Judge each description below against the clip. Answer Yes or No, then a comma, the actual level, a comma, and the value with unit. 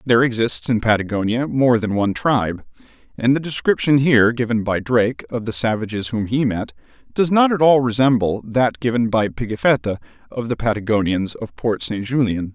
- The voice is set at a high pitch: No, low, 115 Hz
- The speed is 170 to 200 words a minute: Yes, average, 175 wpm